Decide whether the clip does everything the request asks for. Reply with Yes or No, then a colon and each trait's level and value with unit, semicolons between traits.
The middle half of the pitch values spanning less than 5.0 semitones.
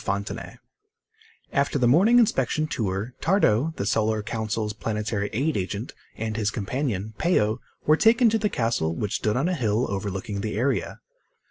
No: wide, 5.4 semitones